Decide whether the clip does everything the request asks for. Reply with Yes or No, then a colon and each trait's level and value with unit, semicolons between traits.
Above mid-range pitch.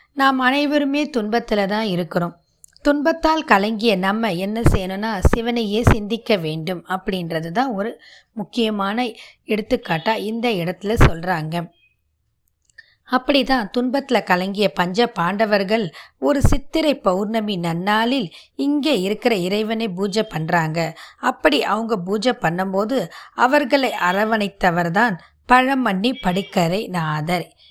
Yes: high, 215 Hz